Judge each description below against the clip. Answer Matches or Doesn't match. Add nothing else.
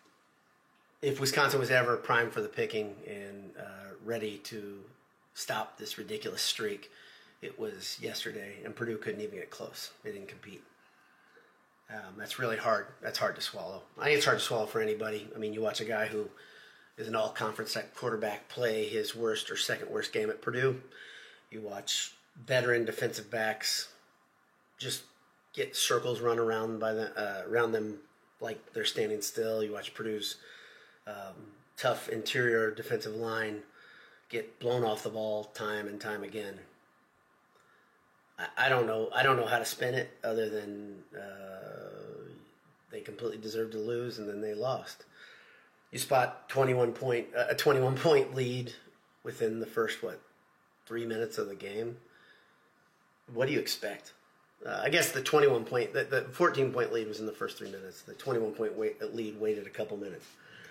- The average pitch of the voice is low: Matches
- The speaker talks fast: Doesn't match